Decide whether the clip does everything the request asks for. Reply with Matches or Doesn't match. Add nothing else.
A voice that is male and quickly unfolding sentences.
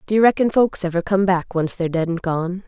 Doesn't match